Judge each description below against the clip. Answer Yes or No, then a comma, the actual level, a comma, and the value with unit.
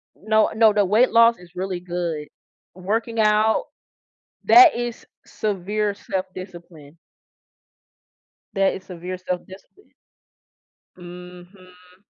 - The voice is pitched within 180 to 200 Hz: Yes, high, 190 Hz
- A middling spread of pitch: Yes, average, 3.2 semitones